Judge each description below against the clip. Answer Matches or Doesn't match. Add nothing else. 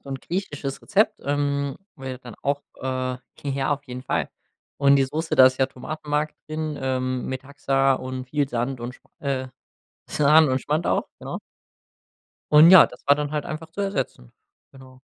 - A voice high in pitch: Doesn't match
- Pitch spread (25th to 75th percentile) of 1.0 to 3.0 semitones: Matches